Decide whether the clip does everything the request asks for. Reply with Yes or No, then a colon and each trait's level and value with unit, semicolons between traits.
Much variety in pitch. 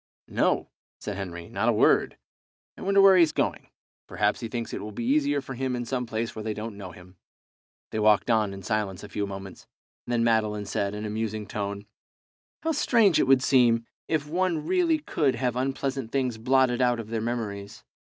No: average, 4.2 semitones